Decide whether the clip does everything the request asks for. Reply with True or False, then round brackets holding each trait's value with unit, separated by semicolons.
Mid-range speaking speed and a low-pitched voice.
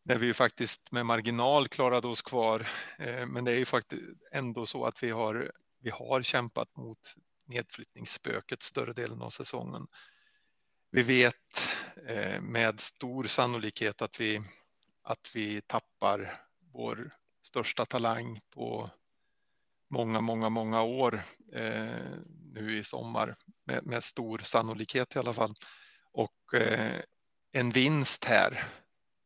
False (120 wpm; 120 Hz)